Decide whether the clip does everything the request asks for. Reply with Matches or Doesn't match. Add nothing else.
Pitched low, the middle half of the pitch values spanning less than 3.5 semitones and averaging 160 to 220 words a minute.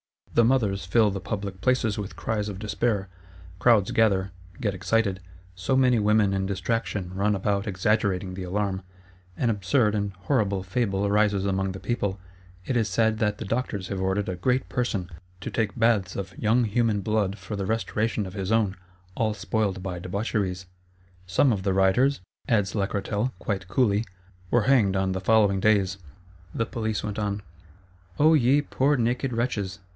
Matches